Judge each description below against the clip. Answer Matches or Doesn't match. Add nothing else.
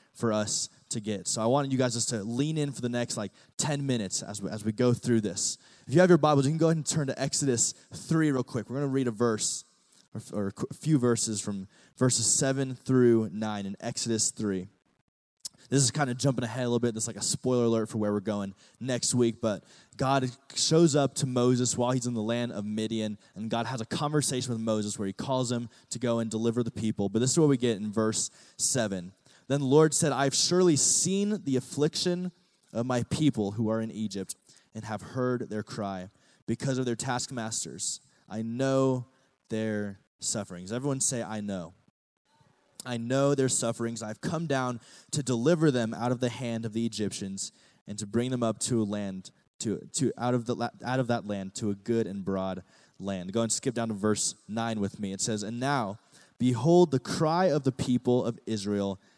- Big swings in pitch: Doesn't match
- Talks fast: Matches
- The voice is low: Matches